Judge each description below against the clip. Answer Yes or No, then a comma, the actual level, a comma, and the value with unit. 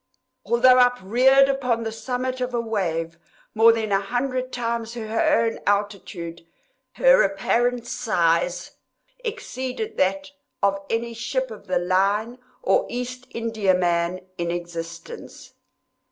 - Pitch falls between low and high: No, high, 230 Hz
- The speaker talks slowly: Yes, slow, 120 wpm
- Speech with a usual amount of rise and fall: Yes, average, 4.9 semitones